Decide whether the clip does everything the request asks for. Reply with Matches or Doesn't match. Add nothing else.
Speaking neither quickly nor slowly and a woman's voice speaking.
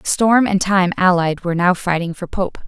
Doesn't match